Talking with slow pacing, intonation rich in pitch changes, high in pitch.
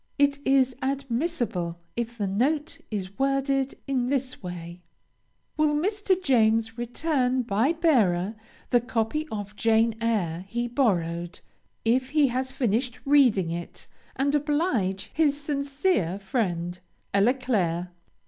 Yes: slow, 120 wpm; wide, 5.9 semitones; high, 245 Hz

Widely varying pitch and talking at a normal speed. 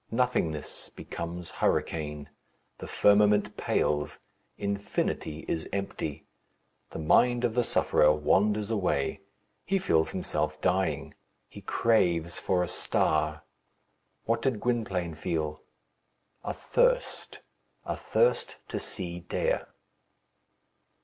No: wide, 5.7 semitones; slow, 105 wpm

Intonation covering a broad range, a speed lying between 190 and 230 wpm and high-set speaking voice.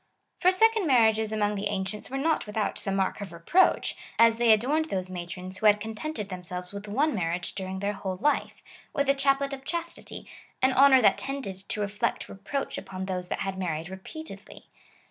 Yes: wide, 6.3 semitones; average, 200 wpm; high, 210 Hz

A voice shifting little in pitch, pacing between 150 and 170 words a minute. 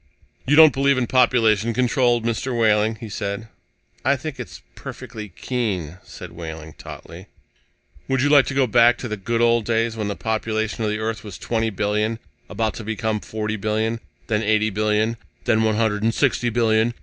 No: narrow, 1.9 semitones; average, 185 wpm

